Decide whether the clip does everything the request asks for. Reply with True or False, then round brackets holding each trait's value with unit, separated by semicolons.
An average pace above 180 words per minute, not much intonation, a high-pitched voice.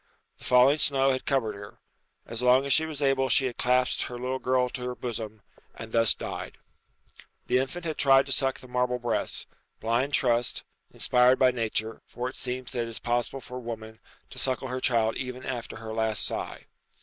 False (200 wpm; 2.1 semitones; 125 Hz)